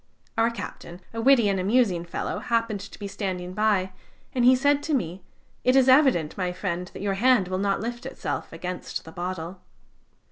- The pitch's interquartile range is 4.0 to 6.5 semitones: Yes, average, 4.9 semitones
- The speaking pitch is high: Yes, high, 200 Hz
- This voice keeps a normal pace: Yes, average, 185 wpm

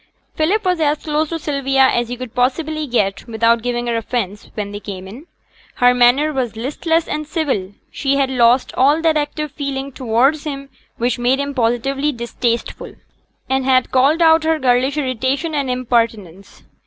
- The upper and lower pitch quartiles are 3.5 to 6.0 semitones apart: Yes, average, 3.8 semitones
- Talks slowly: No, average, 170 wpm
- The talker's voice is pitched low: No, very high, 260 Hz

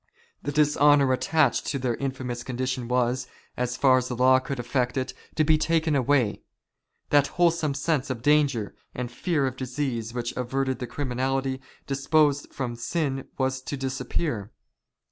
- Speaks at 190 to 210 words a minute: No, average, 160 wpm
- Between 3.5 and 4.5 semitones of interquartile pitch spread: No, narrow, 2.5 semitones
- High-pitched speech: No, low, 130 Hz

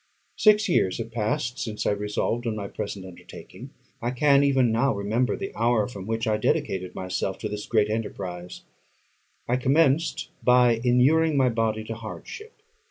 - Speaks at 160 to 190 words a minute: Yes, average, 165 wpm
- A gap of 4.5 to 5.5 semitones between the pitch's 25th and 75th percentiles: No, average, 3.9 semitones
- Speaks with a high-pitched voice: No, low, 115 Hz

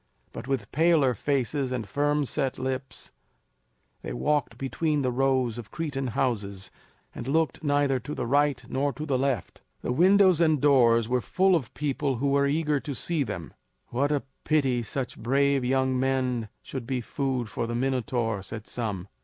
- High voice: No, low, 135 Hz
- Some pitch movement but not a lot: Yes, average, 3.0 semitones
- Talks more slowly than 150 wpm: No, average, 175 wpm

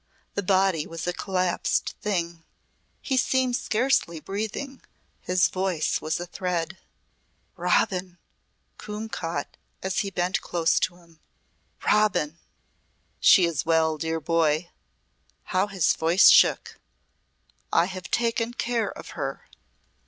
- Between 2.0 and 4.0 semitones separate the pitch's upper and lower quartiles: Yes, average, 3.7 semitones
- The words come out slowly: Yes, slow, 120 wpm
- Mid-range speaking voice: Yes, medium, 180 Hz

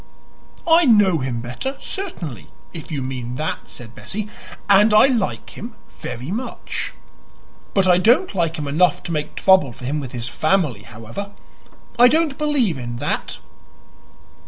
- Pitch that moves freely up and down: Yes, wide, 9.0 semitones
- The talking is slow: No, average, 155 wpm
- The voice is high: No, medium, 170 Hz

